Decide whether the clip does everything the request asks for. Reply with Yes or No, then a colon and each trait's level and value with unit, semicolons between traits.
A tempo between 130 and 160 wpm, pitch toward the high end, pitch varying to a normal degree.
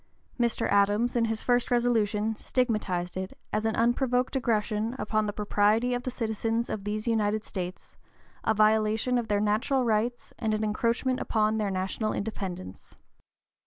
No: average, 155 wpm; high, 220 Hz; narrow, 2.3 semitones